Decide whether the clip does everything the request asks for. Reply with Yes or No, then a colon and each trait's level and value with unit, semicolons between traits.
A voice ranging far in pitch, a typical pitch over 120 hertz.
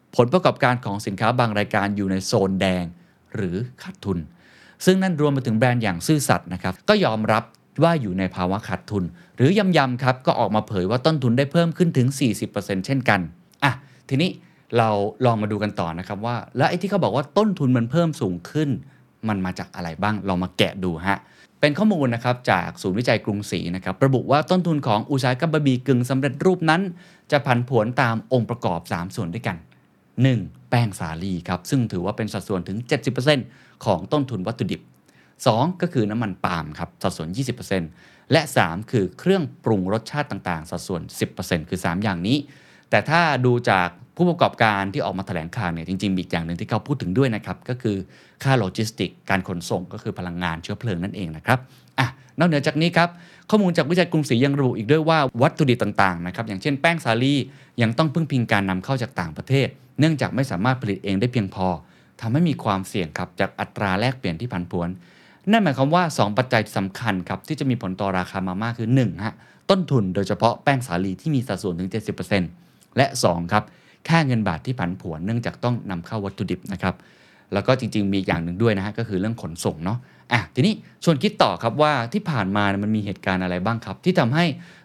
No: wide, 6.3 semitones; low, 115 Hz